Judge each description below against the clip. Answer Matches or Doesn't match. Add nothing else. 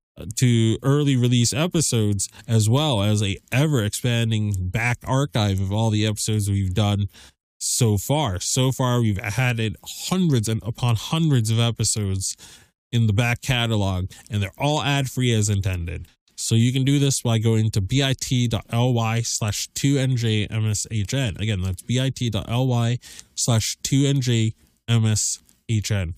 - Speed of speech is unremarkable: Doesn't match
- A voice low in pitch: Matches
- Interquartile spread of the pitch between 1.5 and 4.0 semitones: Matches